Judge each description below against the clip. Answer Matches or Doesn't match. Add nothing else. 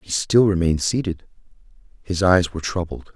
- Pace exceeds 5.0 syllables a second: Matches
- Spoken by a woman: Doesn't match